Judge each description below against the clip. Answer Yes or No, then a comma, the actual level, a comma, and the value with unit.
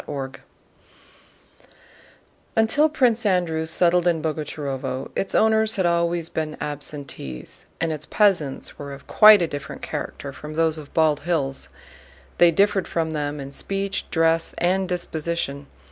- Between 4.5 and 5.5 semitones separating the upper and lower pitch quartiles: No, average, 4.0 semitones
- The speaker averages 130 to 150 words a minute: Yes, average, 140 wpm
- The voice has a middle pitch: Yes, medium, 165 Hz